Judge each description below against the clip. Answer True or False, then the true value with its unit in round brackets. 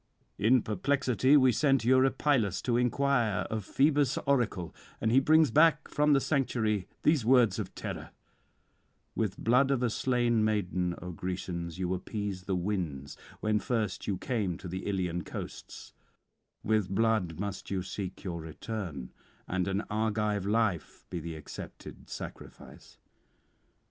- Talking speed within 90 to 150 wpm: True (140 wpm)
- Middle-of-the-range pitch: False (110 Hz)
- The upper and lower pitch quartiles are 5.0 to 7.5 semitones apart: True (5.4 semitones)